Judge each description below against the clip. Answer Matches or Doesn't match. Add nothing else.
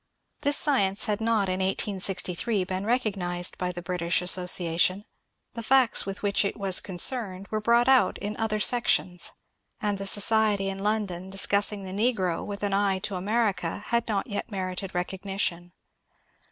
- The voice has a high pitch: Matches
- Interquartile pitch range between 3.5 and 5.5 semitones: Doesn't match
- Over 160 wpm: Doesn't match